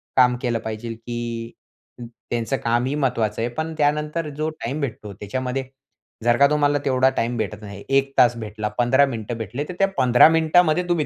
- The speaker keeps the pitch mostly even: No, average, 4.0 semitones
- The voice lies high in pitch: No, low, 125 Hz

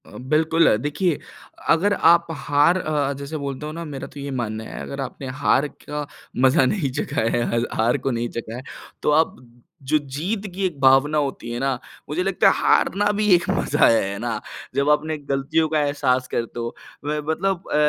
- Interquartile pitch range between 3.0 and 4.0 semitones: Yes, average, 3.6 semitones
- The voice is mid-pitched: Yes, medium, 145 Hz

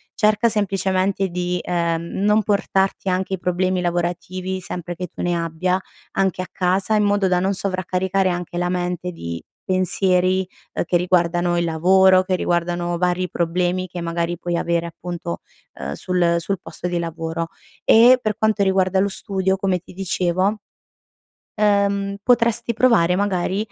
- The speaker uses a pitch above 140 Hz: Yes, medium, 185 Hz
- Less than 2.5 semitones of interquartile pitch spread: Yes, narrow, 1.9 semitones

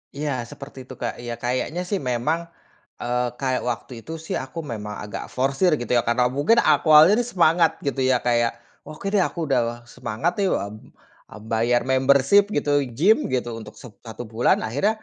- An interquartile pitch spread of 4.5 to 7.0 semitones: Yes, average, 4.8 semitones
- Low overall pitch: Yes, low, 130 Hz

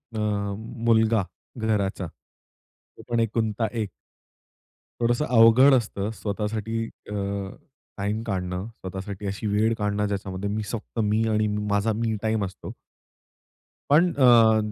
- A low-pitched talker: Yes, low, 110 Hz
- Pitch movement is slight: Yes, narrow, 2.0 semitones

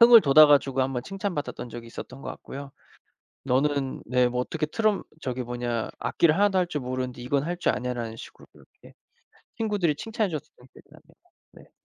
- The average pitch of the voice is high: No, medium, 140 Hz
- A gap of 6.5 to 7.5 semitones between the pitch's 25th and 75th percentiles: No, wide, 5.9 semitones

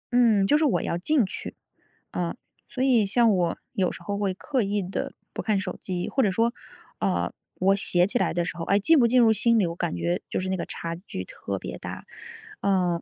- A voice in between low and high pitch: No, high, 200 Hz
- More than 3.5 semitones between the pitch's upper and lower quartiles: Yes, average, 4.5 semitones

